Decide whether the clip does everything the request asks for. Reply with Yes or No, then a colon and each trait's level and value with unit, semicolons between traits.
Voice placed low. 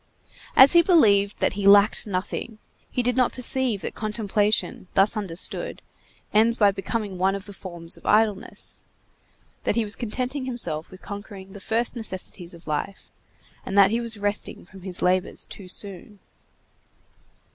No: high, 205 Hz